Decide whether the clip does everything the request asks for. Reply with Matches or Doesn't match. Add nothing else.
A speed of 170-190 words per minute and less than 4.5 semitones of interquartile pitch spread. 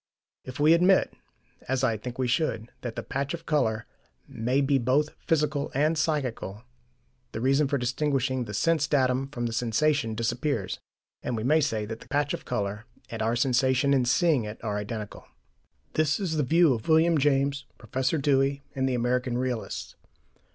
Matches